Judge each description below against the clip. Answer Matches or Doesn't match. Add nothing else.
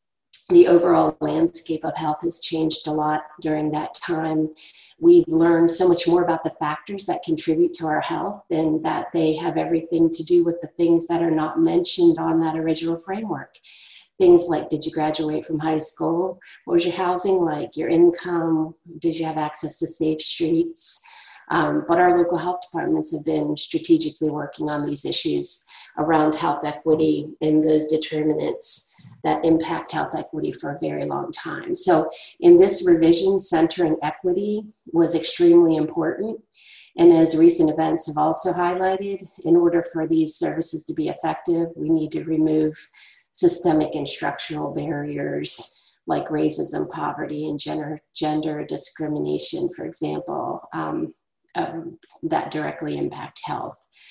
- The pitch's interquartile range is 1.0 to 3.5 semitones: Doesn't match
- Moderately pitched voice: Matches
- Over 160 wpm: Doesn't match